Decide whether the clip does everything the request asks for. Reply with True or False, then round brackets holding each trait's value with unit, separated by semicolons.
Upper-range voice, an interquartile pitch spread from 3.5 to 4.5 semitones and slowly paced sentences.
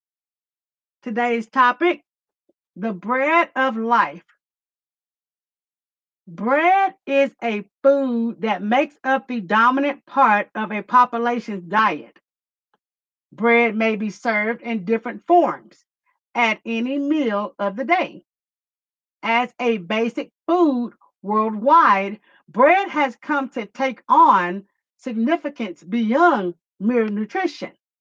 True (235 Hz; 4.2 semitones; 105 wpm)